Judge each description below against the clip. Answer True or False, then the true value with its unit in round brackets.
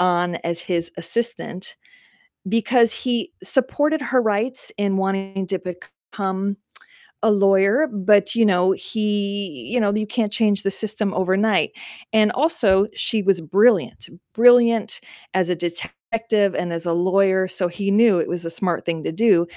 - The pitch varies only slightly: False (3.4 semitones)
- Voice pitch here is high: True (200 Hz)